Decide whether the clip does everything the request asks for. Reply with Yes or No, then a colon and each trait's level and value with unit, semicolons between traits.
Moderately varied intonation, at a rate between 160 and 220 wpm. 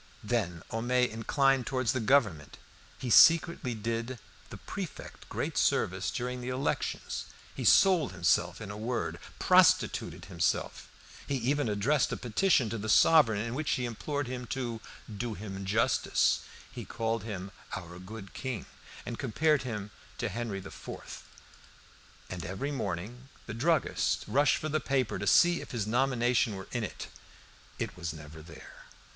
No: average, 4.4 semitones; average, 150 wpm